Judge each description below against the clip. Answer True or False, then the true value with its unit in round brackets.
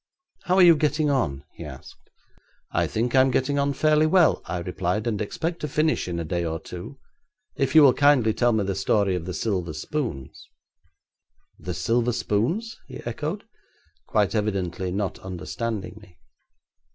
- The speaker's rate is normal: True (165 wpm)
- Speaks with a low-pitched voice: True (115 Hz)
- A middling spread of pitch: False (7.6 semitones)